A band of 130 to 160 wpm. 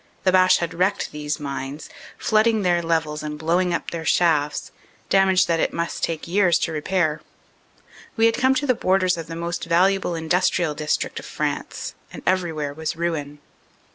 No: average, 175 wpm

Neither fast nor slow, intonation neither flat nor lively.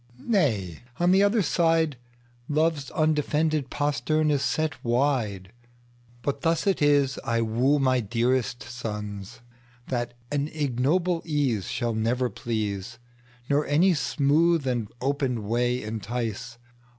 No: slow, 100 wpm; average, 3.9 semitones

